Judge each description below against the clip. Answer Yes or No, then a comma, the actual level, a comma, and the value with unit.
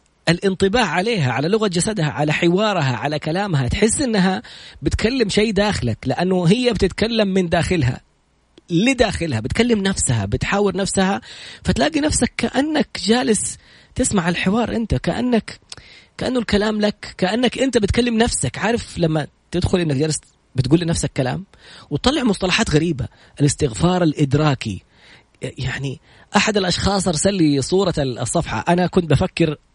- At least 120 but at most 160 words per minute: Yes, average, 125 wpm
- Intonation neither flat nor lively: No, wide, 6.5 semitones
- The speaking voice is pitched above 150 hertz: Yes, medium, 180 Hz